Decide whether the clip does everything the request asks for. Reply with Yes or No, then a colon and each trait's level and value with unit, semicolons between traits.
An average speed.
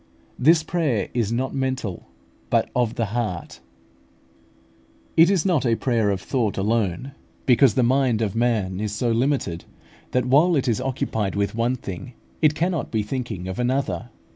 Yes: average, 165 wpm